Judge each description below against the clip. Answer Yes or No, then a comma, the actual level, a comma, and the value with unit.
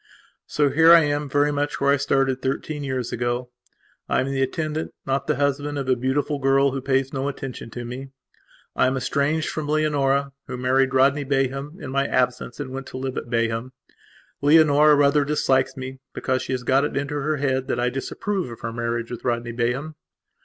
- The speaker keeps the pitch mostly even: Yes, narrow, 2.1 semitones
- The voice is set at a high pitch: No, low, 135 Hz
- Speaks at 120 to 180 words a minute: No, average, 200 wpm